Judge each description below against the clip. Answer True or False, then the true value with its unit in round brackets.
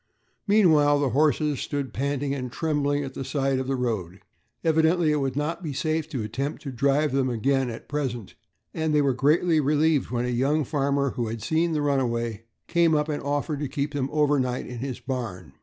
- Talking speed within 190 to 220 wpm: True (200 wpm)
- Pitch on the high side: False (140 Hz)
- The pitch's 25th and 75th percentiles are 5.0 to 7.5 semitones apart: False (2.9 semitones)